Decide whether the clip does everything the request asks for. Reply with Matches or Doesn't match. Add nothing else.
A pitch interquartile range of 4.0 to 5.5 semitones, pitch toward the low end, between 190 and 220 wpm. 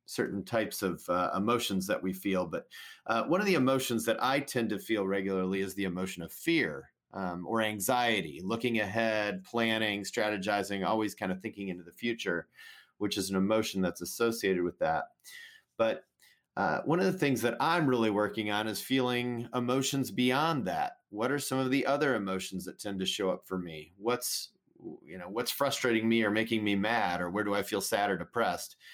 Matches